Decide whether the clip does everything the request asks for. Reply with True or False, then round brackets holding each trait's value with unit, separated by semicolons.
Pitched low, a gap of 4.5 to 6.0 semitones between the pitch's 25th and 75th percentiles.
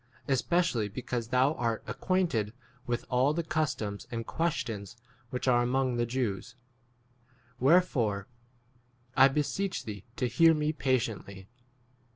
True (125 Hz; 4.9 semitones)